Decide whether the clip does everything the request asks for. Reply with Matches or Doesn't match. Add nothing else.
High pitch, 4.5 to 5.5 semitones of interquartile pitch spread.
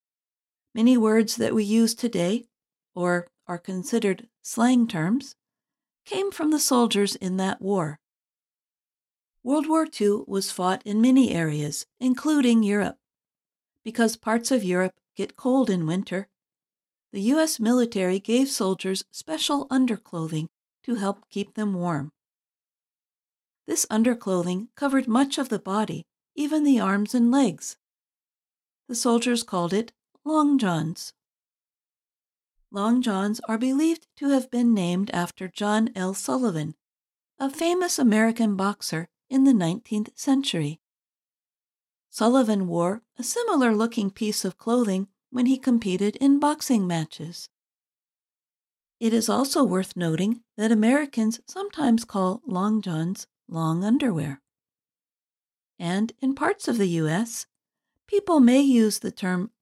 Matches